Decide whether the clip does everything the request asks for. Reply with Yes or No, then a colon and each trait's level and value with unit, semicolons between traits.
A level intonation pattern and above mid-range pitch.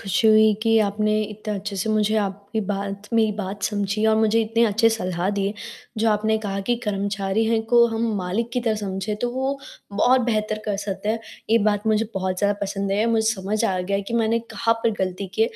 Yes: narrow, 2.1 semitones; high, 215 Hz